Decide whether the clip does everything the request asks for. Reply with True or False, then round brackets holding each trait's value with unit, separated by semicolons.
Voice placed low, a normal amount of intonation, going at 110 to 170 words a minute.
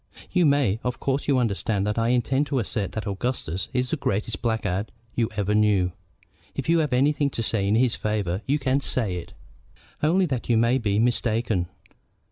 False (115 Hz; 4.2 semitones; 190 wpm)